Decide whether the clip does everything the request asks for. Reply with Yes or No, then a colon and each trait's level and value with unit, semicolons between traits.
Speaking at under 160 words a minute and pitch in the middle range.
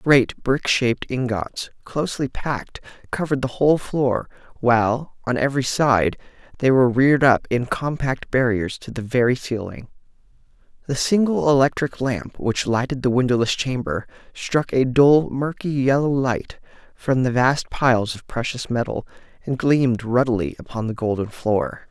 No: average, 150 wpm; low, 125 Hz